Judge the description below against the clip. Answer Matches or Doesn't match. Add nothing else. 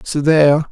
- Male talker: Matches